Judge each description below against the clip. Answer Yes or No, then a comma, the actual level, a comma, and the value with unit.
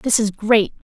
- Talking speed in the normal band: Yes, average, 180 wpm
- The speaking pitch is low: No, high, 215 Hz